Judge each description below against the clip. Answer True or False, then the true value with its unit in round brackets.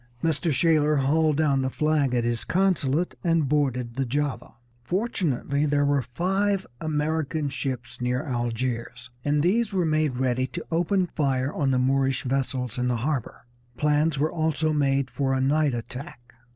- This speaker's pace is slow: False (160 wpm)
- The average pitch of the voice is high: False (145 Hz)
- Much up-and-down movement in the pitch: False (3.5 semitones)